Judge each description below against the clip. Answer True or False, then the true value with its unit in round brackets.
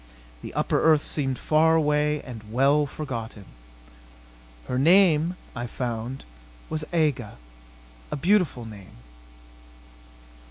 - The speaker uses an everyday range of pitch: True (4.5 semitones)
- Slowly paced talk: True (105 wpm)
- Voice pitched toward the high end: False (145 Hz)